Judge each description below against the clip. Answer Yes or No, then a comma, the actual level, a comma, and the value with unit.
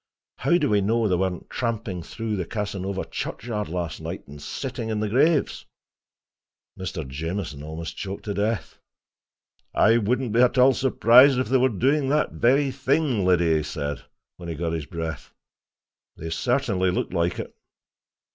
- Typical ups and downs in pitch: No, wide, 6.7 semitones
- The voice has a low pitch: Yes, low, 105 Hz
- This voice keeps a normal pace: Yes, average, 165 wpm